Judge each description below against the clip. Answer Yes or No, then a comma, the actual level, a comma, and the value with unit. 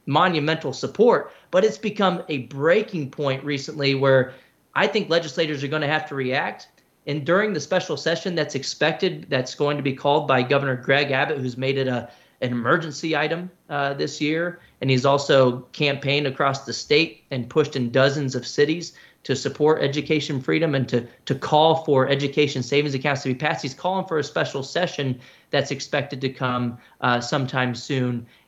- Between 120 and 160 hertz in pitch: Yes, medium, 140 Hz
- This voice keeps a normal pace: Yes, average, 180 wpm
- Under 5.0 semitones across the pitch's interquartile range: Yes, average, 2.8 semitones